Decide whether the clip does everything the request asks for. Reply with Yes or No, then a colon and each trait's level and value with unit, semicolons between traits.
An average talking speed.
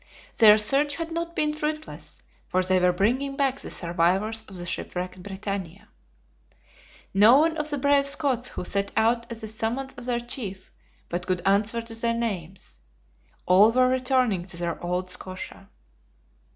Yes: average, 165 wpm